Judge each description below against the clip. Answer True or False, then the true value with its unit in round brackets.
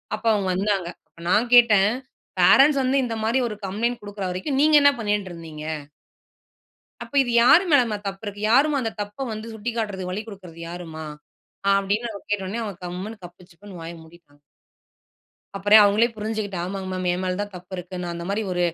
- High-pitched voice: True (205 Hz)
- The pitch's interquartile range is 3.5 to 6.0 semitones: True (3.9 semitones)